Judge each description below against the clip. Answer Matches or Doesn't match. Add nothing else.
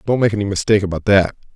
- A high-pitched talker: Doesn't match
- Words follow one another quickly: Matches